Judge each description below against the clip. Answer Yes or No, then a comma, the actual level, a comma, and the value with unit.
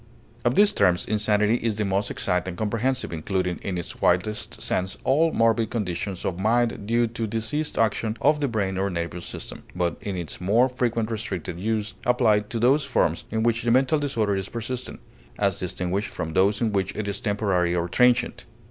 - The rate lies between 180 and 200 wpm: Yes, average, 190 wpm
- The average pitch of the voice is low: Yes, low, 105 Hz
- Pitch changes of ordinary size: Yes, average, 3.9 semitones